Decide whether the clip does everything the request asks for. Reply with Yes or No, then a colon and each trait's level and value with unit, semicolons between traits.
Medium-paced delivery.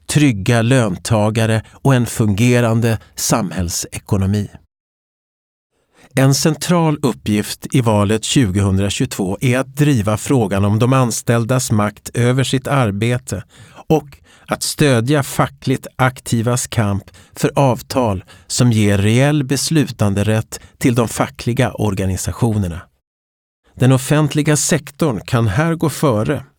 No: slow, 105 wpm